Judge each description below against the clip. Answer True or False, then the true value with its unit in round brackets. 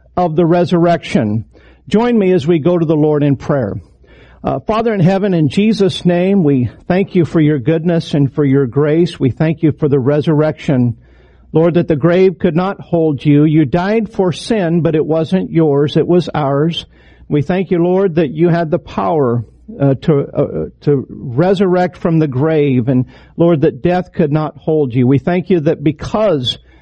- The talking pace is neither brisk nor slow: True (190 wpm)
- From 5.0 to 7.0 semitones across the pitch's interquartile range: False (3.9 semitones)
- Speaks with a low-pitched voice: False (160 Hz)